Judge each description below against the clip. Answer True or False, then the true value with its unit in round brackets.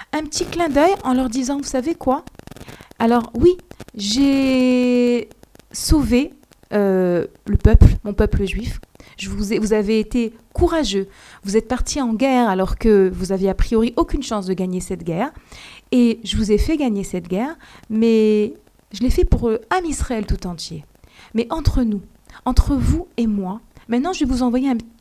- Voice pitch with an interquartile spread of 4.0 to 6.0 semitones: True (4.6 semitones)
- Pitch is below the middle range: False (235 Hz)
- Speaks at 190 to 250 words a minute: False (180 wpm)